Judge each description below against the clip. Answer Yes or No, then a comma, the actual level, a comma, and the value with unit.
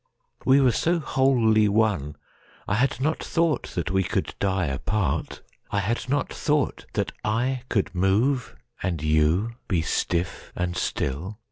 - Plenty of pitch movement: Yes, wide, 6.1 semitones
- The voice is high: No, low, 105 Hz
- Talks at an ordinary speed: No, slow, 130 wpm